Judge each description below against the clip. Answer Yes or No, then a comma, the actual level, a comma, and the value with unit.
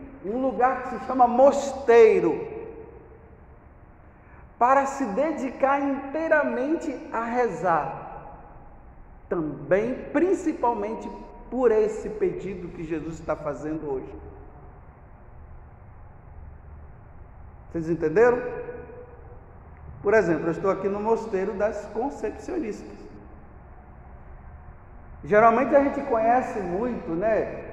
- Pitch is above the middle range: Yes, high, 220 Hz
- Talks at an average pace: No, slow, 85 wpm